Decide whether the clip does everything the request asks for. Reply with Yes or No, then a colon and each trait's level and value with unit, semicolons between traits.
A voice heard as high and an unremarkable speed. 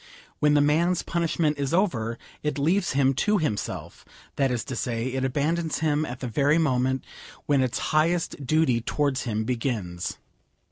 No: medium, 140 Hz; average, 160 wpm